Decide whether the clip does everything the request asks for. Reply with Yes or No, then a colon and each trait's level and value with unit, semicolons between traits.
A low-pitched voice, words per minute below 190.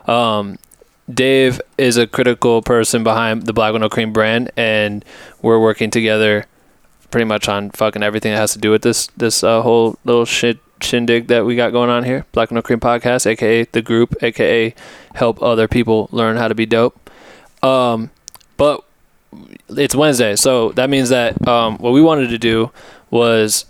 Yes: low, 115 Hz; average, 175 wpm